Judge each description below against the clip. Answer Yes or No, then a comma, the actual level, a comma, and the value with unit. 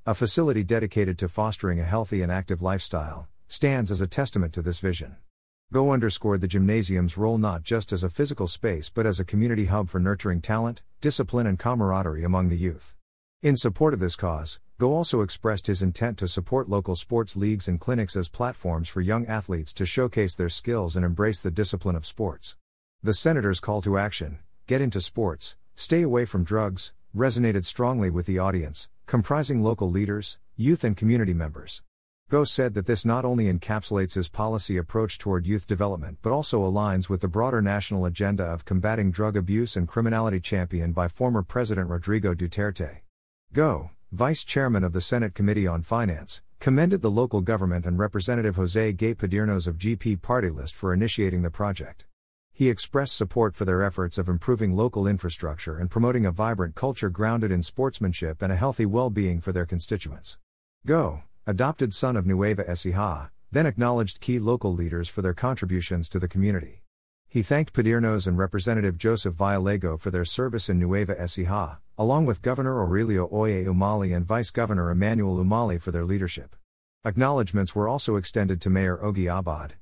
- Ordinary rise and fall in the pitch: Yes, average, 4.0 semitones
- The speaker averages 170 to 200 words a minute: Yes, average, 175 wpm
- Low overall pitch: Yes, low, 100 Hz